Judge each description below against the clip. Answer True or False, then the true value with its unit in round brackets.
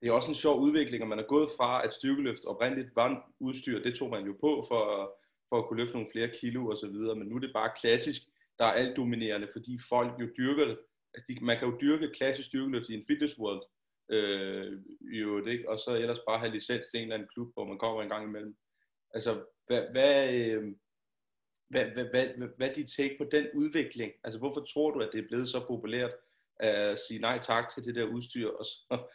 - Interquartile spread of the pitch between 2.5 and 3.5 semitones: False (3.9 semitones)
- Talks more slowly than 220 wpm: False (225 wpm)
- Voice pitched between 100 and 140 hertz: True (120 Hz)